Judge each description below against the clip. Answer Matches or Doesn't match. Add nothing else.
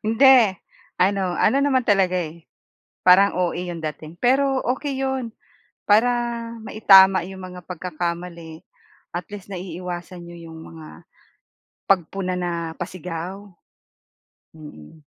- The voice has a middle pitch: Matches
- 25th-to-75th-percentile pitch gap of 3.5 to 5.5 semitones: Doesn't match